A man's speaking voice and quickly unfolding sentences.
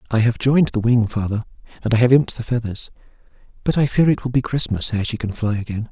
Yes: male; fast, 245 wpm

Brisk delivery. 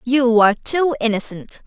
No: average, 145 wpm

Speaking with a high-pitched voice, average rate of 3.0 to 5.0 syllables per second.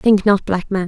Yes: high, 195 Hz; 4.6 syllables/s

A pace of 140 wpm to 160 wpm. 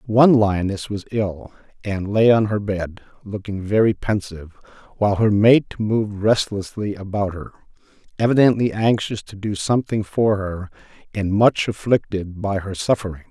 Yes: average, 145 wpm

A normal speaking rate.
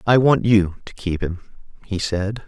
Yes: average, 195 wpm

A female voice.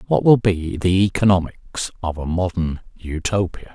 No: male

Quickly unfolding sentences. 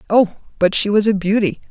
Yes: fast, 210 wpm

